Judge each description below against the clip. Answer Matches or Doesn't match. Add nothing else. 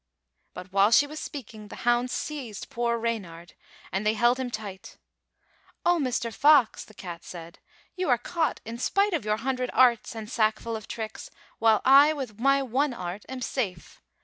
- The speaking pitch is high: Matches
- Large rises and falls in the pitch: Doesn't match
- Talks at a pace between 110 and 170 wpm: Doesn't match